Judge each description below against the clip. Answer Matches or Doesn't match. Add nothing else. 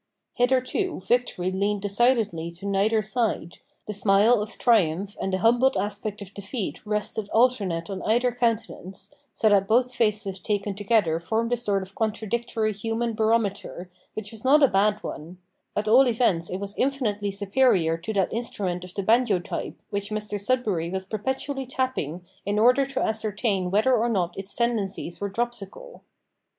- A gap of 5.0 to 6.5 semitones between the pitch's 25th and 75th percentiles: Doesn't match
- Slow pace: Doesn't match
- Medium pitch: Doesn't match